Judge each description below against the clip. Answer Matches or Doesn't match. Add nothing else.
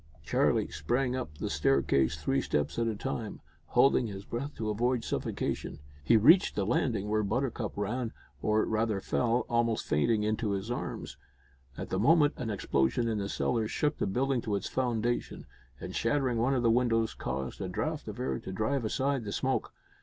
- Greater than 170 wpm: Matches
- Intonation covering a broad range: Doesn't match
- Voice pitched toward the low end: Matches